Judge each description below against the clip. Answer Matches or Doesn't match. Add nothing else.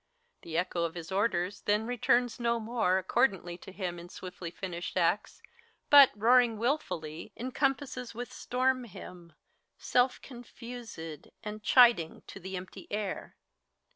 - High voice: Matches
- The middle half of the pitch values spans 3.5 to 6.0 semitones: Matches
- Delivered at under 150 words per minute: Matches